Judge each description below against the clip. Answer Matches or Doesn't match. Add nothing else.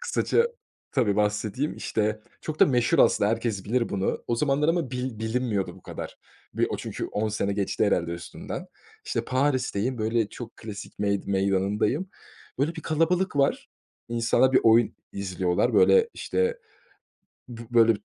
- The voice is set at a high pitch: Doesn't match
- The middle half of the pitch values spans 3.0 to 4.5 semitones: Doesn't match